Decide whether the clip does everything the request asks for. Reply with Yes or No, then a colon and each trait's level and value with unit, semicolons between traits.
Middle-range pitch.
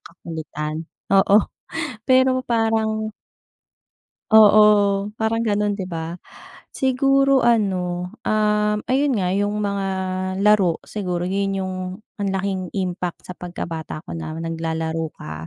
No: high, 195 Hz